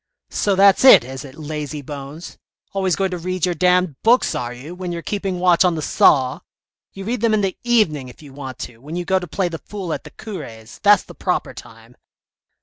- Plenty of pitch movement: No, average, 5.0 semitones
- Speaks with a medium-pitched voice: Yes, medium, 175 Hz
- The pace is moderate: No, fast, 230 wpm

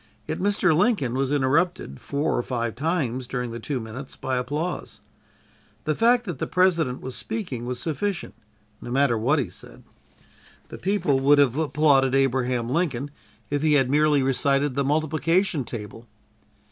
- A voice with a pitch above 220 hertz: No, medium, 140 Hz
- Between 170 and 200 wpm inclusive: No, average, 160 wpm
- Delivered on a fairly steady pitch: No, average, 3.9 semitones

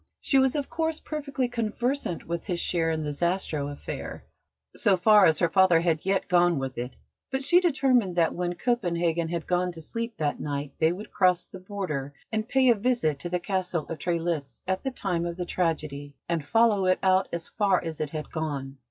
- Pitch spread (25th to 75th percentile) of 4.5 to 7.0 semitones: Yes, average, 5.1 semitones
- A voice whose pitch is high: No, medium, 175 Hz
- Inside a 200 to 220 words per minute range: Yes, fast, 205 wpm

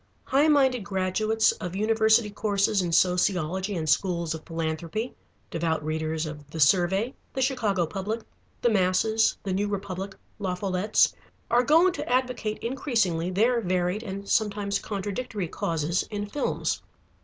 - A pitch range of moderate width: Yes, average, 3.9 semitones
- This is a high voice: Yes, high, 200 Hz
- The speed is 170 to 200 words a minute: No, average, 140 wpm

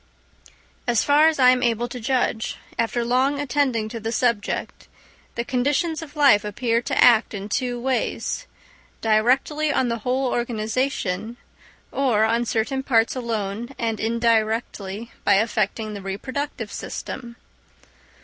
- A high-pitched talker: Yes, high, 235 Hz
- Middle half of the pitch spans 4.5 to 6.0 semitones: No, average, 3.0 semitones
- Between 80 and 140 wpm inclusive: Yes, slow, 135 wpm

